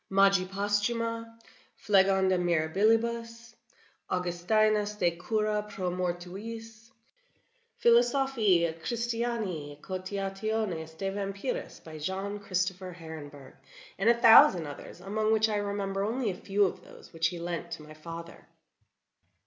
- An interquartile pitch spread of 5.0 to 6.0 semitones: No, average, 3.8 semitones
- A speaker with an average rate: No, slow, 120 wpm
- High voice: Yes, high, 195 Hz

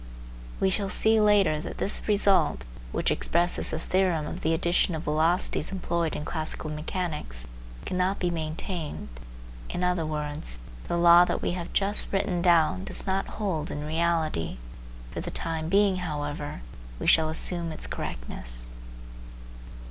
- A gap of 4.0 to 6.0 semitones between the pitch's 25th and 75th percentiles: No, average, 3.2 semitones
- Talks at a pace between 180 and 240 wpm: No, average, 150 wpm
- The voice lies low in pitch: No, medium, 170 Hz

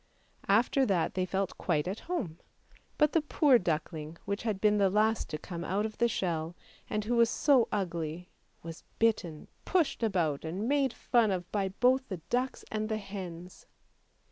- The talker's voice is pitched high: Yes, high, 200 Hz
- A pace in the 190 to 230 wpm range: No, average, 180 wpm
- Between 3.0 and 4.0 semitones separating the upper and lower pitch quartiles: No, average, 4.8 semitones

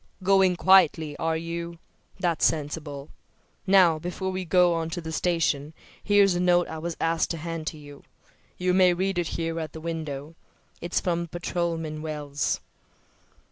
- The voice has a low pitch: No, medium, 165 Hz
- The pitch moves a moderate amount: No, narrow, 2.1 semitones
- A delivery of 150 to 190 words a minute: Yes, average, 155 wpm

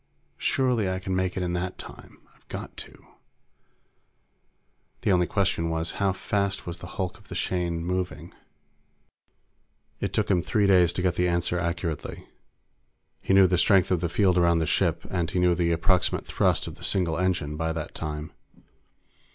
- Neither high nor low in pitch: No, very low, 90 Hz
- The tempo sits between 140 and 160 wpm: No, average, 175 wpm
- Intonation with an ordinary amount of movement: No, narrow, 1.7 semitones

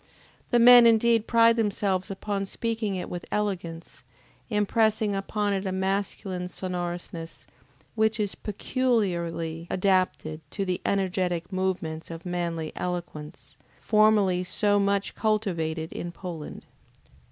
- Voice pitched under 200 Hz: Yes, high, 190 Hz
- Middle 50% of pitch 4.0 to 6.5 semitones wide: No, average, 3.2 semitones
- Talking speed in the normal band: No, slow, 115 wpm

